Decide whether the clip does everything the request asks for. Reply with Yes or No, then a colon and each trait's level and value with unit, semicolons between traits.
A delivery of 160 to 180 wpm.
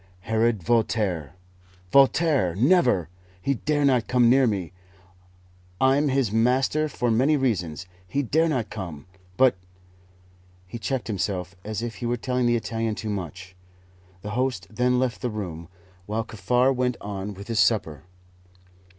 No: average, 150 wpm